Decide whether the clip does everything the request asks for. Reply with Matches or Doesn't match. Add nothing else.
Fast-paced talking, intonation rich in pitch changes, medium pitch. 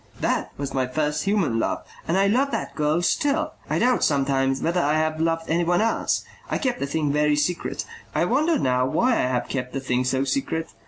Matches